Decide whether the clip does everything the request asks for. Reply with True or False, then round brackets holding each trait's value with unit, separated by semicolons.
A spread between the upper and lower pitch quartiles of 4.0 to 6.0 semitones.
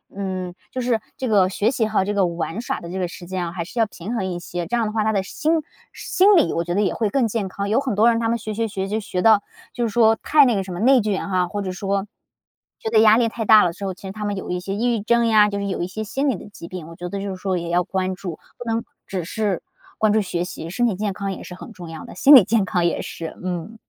False (3.5 semitones)